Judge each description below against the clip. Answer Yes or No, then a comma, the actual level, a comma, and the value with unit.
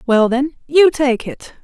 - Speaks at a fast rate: No, average, 185 wpm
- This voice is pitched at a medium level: No, very high, 270 Hz